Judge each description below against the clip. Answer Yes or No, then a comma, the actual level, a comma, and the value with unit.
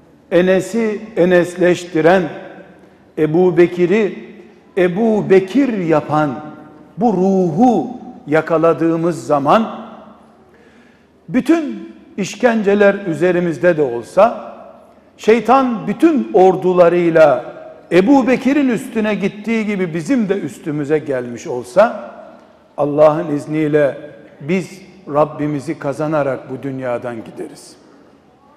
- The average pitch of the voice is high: No, medium, 180 Hz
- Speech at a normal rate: No, slow, 80 wpm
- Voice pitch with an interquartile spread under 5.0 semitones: No, wide, 5.4 semitones